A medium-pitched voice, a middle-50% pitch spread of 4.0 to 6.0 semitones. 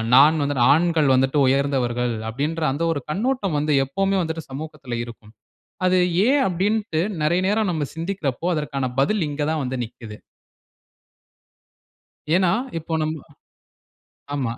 Yes: medium, 155 Hz; average, 4.5 semitones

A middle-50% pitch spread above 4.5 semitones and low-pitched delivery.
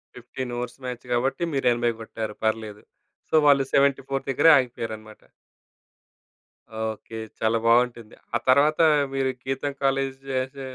No: average, 2.9 semitones; low, 125 Hz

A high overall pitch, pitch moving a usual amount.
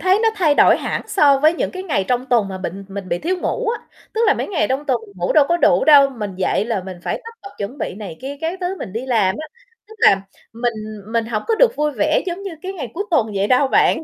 No: very high, 270 Hz; wide, 9.0 semitones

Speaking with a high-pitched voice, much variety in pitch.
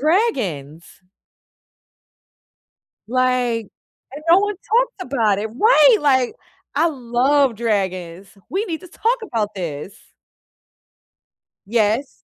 Yes: very high, 250 Hz; wide, 8.0 semitones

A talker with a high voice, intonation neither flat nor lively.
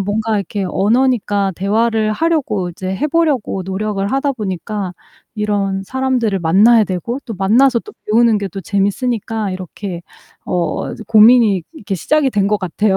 Yes: high, 210 Hz; average, 3.5 semitones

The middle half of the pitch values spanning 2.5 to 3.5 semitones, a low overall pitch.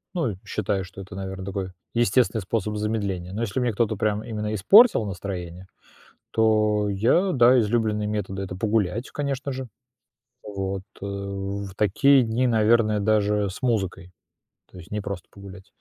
Yes: average, 2.8 semitones; low, 105 Hz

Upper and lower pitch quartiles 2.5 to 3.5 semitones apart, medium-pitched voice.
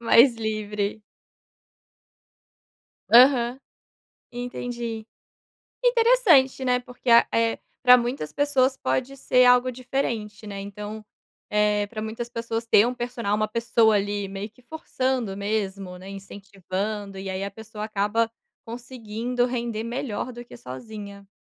No: average, 3.2 semitones; high, 225 Hz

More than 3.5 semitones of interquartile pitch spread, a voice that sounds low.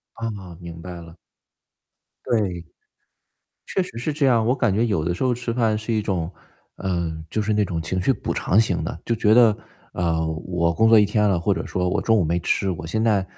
Yes: average, 4.5 semitones; low, 100 Hz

